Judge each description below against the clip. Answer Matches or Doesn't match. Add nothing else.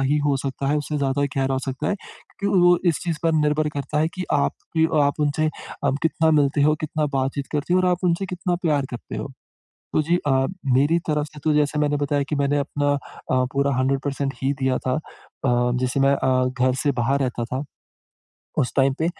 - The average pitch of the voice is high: Doesn't match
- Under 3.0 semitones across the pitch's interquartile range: Matches